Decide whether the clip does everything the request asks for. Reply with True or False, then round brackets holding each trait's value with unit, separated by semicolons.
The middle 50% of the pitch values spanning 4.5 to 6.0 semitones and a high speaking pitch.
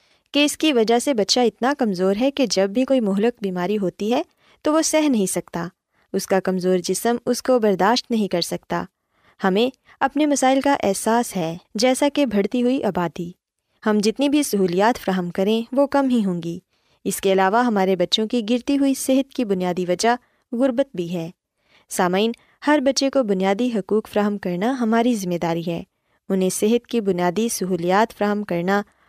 True (5.1 semitones; 220 Hz)